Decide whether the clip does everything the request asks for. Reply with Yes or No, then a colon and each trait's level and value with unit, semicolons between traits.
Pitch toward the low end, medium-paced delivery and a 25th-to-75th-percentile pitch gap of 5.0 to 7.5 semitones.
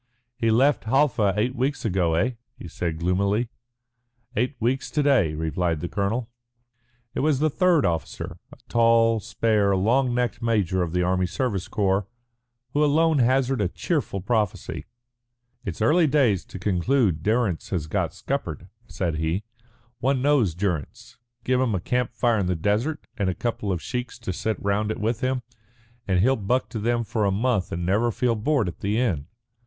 Yes: low, 110 Hz; average, 175 wpm; average, 5.3 semitones